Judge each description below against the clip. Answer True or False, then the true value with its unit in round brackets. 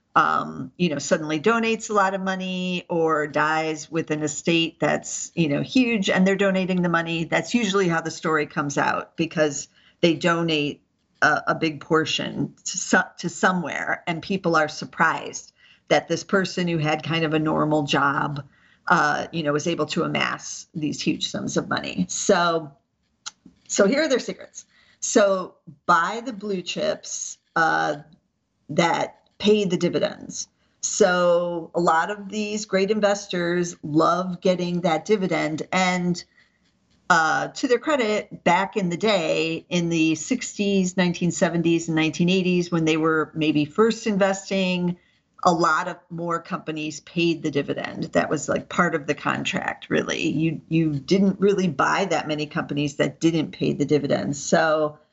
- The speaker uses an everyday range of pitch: True (3.5 semitones)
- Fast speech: False (155 wpm)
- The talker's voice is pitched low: False (170 Hz)